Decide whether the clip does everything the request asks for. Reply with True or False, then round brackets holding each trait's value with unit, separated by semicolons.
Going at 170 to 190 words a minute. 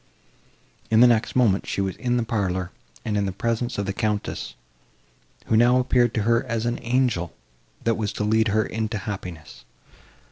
True (180 wpm)